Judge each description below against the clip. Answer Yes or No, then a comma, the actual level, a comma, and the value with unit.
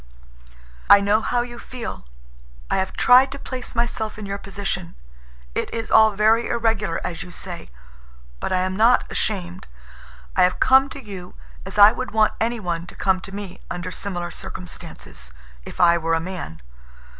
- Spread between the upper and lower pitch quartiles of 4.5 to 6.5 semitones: No, average, 4.1 semitones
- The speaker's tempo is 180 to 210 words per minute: No, average, 170 wpm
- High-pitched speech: Yes, high, 200 Hz